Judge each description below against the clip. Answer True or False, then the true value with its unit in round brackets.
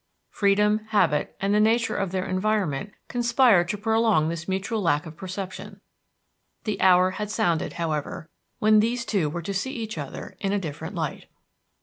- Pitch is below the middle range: False (195 Hz)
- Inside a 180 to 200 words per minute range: False (165 wpm)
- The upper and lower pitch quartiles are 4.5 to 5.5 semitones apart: False (3.9 semitones)